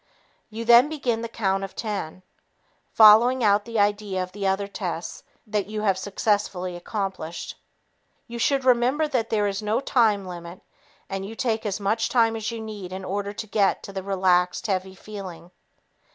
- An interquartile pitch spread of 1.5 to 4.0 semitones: Yes, average, 2.8 semitones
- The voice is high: Yes, high, 205 Hz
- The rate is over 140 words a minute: Yes, average, 165 wpm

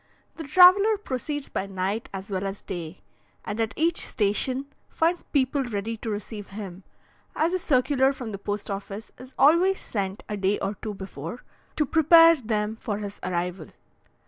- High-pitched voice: Yes, high, 220 Hz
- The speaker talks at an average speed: Yes, average, 170 wpm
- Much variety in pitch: Yes, wide, 6.5 semitones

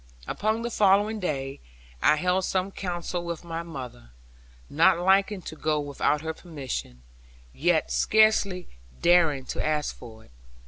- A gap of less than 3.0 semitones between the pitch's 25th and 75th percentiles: No, average, 4.3 semitones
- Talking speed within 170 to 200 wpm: No, average, 140 wpm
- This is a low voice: No, medium, 170 Hz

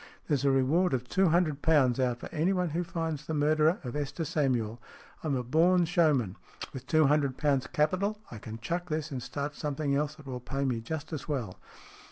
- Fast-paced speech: Yes, fast, 210 wpm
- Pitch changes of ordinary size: Yes, average, 3.6 semitones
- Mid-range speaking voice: Yes, medium, 150 Hz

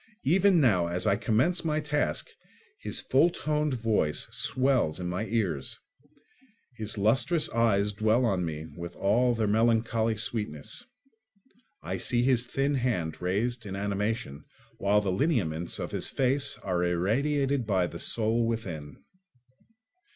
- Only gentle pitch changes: No, wide, 5.5 semitones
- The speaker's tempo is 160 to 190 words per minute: No, slow, 135 wpm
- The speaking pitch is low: Yes, low, 110 Hz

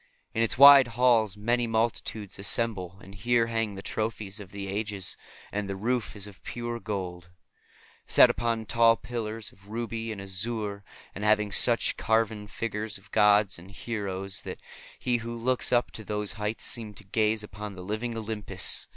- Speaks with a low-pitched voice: Yes, low, 110 Hz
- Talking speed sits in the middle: Yes, average, 170 wpm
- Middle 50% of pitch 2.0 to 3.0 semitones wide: Yes, narrow, 2.4 semitones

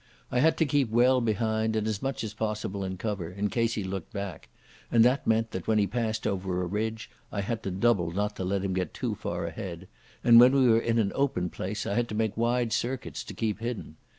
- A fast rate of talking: Yes, fast, 245 wpm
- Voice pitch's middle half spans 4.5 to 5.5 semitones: No, average, 3.1 semitones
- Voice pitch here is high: No, low, 110 Hz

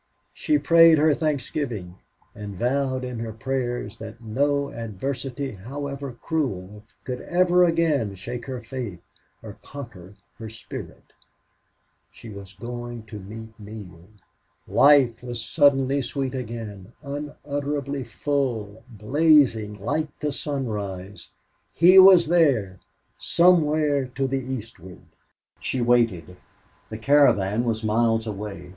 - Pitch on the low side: Yes, low, 120 Hz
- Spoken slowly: Yes, slow, 115 wpm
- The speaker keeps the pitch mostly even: No, average, 4.9 semitones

